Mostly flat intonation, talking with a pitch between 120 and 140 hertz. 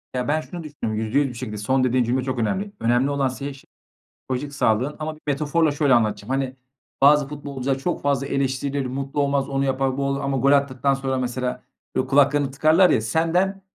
Yes: narrow, 2.0 semitones; low, 135 Hz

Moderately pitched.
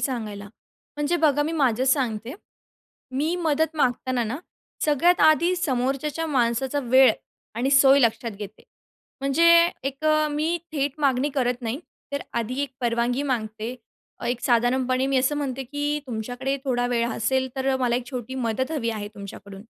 No: very high, 260 Hz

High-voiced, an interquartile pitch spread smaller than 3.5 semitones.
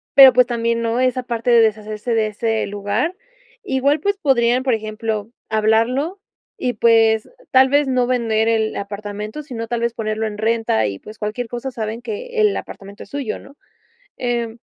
Yes: high, 230 Hz; average, 2.8 semitones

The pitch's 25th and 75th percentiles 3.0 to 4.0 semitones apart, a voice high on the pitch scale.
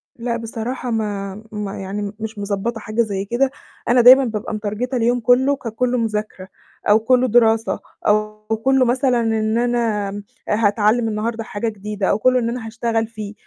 No: narrow, 2.4 semitones; high, 225 Hz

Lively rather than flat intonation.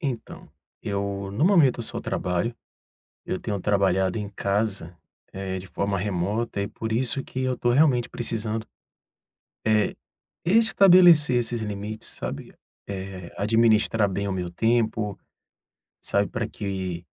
No: average, 3.4 semitones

